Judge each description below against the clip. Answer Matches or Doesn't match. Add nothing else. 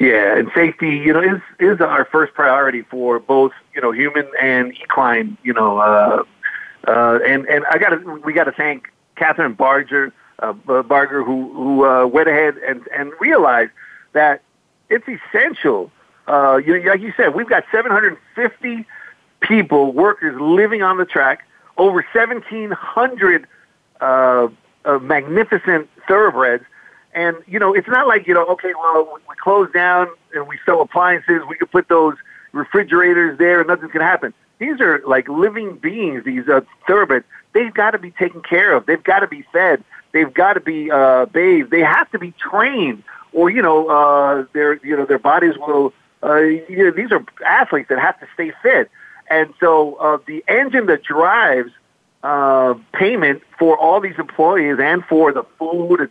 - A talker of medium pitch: Matches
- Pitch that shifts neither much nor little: Matches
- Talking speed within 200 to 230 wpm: Doesn't match